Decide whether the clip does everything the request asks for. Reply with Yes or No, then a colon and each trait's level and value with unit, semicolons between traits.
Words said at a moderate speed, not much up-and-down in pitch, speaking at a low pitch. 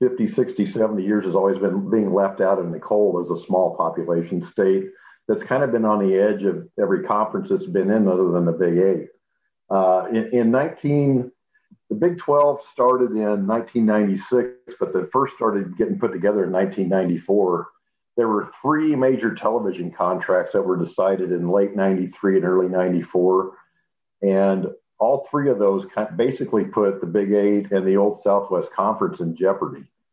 No: average, 175 wpm; average, 3.7 semitones; low, 100 Hz